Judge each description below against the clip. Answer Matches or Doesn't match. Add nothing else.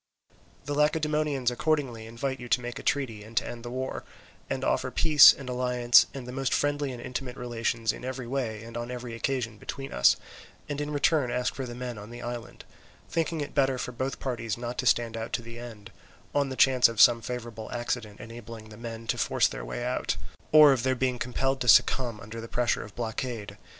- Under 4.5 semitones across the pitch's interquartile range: Matches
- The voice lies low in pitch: Matches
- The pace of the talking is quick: Matches